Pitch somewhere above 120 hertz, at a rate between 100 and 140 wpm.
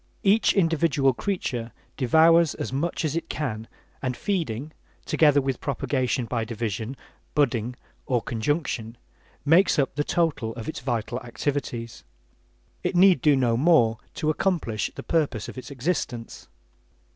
Yes: low, 135 Hz; slow, 135 wpm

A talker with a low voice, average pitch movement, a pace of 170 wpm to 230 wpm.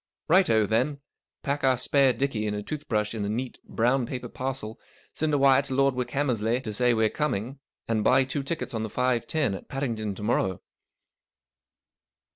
Yes: low, 125 Hz; average, 3.8 semitones; average, 190 wpm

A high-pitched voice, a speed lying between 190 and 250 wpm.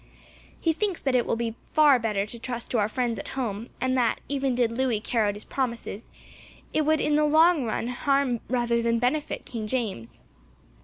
Yes: high, 245 Hz; average, 200 wpm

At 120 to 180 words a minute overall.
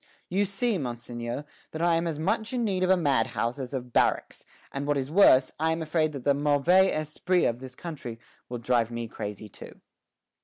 No: average, 200 wpm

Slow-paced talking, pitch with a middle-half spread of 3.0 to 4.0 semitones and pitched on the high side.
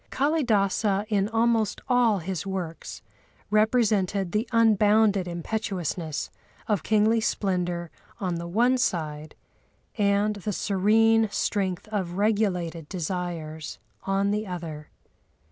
Yes: slow, 105 wpm; average, 3.7 semitones; high, 200 Hz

